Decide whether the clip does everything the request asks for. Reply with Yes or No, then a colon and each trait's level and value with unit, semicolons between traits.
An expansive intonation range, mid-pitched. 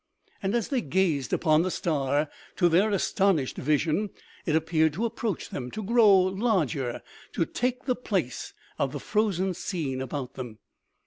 Yes: wide, 6.0 semitones; medium, 175 Hz